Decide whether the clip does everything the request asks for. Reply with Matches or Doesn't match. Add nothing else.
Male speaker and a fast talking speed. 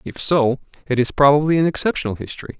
Doesn't match